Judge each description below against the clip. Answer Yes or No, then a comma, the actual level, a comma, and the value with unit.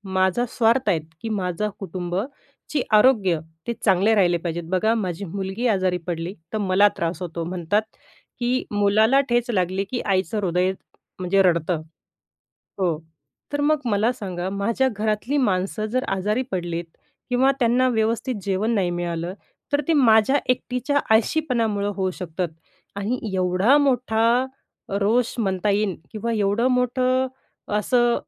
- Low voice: No, high, 205 Hz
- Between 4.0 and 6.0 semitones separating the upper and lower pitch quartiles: Yes, average, 4.6 semitones